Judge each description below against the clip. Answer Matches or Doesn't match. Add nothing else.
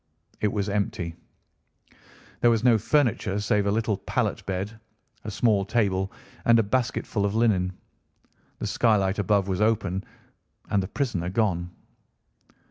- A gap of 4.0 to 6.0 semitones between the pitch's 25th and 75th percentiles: Doesn't match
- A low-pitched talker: Matches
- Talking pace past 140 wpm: Doesn't match